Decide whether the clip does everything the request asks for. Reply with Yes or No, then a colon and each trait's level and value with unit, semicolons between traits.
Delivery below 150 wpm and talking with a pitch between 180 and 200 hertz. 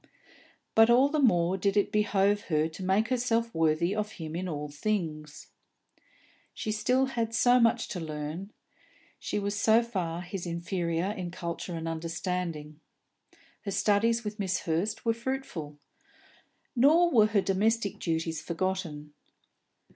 Yes: average, 140 wpm; high, 190 Hz